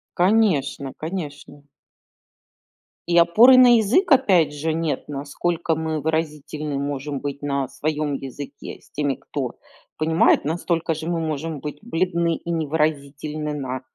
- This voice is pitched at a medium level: Yes, medium, 155 Hz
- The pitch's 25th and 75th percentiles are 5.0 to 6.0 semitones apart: No, average, 2.8 semitones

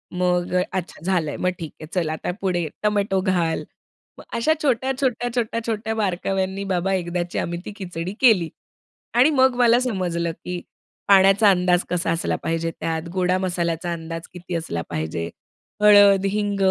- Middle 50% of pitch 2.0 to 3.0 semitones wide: No, average, 3.4 semitones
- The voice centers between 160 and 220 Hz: Yes, medium, 185 Hz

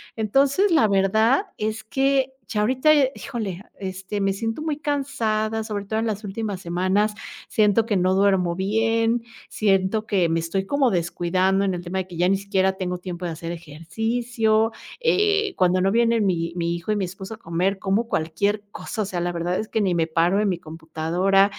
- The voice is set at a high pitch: Yes, high, 200 Hz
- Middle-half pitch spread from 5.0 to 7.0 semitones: No, average, 3.8 semitones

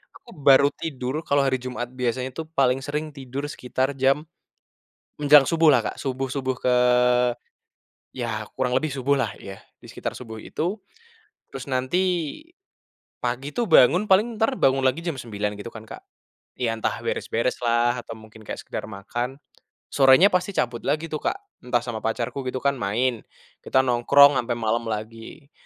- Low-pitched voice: Yes, low, 130 Hz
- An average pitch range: Yes, average, 3.0 semitones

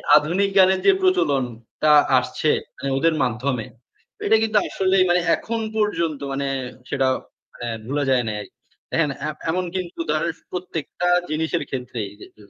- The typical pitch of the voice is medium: Yes, medium, 155 Hz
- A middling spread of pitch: No, wide, 5.7 semitones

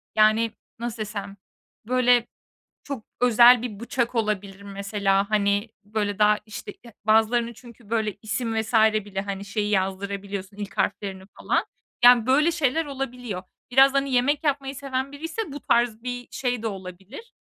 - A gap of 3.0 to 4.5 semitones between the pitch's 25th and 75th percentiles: Yes, average, 3.6 semitones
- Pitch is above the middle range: Yes, high, 225 Hz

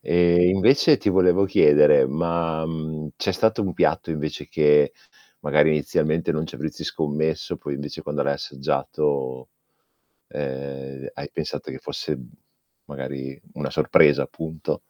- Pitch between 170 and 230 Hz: No, very low, 75 Hz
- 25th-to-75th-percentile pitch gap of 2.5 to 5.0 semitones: Yes, average, 2.8 semitones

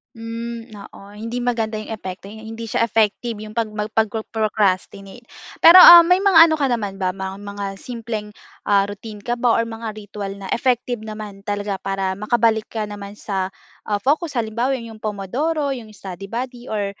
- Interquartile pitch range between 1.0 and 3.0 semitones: Yes, average, 2.7 semitones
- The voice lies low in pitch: No, high, 220 Hz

